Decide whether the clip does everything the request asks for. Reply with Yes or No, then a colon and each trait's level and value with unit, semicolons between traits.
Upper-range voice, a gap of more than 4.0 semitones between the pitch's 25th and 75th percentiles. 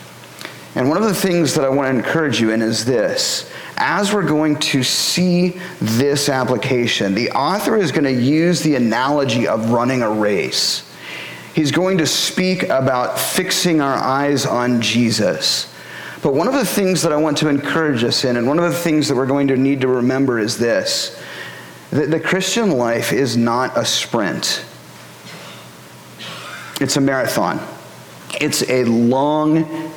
No: medium, 140 Hz; wide, 5.4 semitones